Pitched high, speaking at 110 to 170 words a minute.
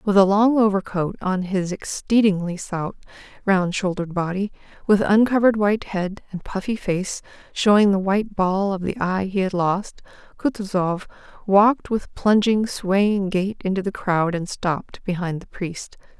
Yes: high, 195 Hz; average, 155 wpm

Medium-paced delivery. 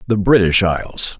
Yes: average, 150 wpm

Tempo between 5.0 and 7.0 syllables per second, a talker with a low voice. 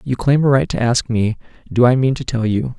Yes: 5.5 syllables/s; low, 120 Hz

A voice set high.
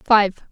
Yes: high, 210 Hz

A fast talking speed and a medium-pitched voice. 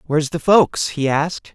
No: average, 195 wpm; medium, 155 Hz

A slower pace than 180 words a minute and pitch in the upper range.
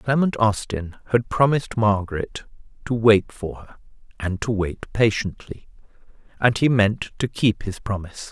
No: average, 145 wpm; low, 110 Hz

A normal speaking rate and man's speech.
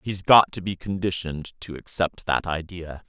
Yes: average, 175 wpm; male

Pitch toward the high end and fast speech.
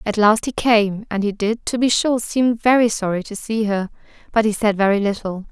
Yes: high, 215 Hz; fast, 230 wpm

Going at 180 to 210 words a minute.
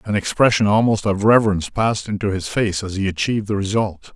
Yes: average, 200 wpm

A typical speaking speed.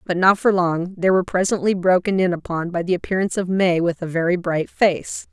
No: fast, 225 wpm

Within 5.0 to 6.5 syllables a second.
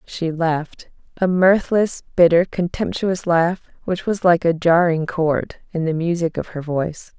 No: 4.2 syllables/s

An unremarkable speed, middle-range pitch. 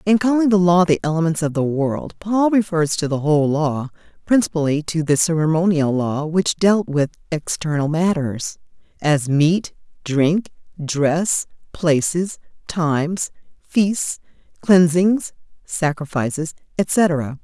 No: slow, 120 wpm; medium, 165 Hz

